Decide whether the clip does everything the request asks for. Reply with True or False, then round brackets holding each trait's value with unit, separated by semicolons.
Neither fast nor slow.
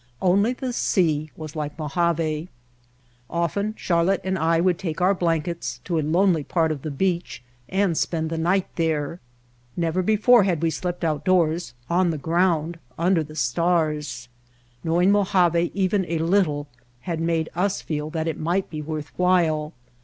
True (160 wpm)